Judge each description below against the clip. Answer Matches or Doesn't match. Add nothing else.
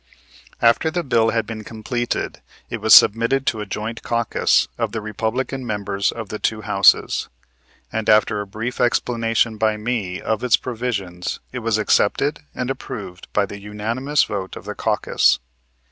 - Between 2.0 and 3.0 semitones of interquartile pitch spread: Matches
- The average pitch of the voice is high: Doesn't match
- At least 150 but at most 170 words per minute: Matches